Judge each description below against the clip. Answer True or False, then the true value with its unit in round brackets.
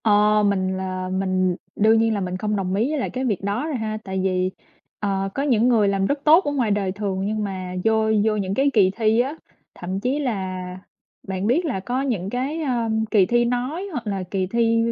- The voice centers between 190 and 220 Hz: True (210 Hz)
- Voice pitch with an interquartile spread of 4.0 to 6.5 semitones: True (4.3 semitones)